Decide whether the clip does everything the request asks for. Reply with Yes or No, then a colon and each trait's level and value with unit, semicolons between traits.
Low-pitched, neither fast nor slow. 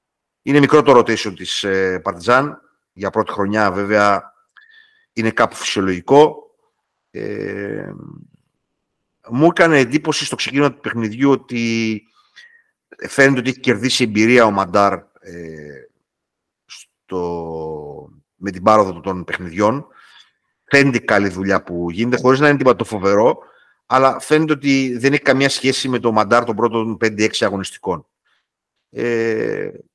Yes: low, 120 Hz; average, 130 wpm